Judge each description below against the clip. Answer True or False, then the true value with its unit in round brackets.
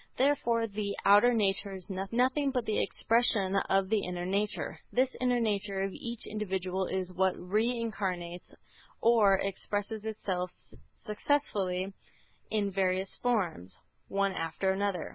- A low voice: False (200 Hz)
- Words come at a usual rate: False (130 wpm)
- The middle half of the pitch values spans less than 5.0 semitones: True (3.2 semitones)